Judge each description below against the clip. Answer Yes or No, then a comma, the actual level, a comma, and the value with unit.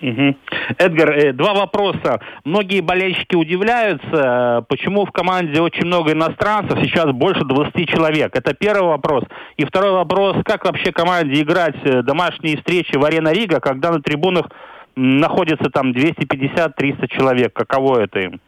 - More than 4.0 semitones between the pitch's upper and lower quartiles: Yes, average, 4.7 semitones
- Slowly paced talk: No, average, 135 wpm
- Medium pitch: Yes, medium, 165 Hz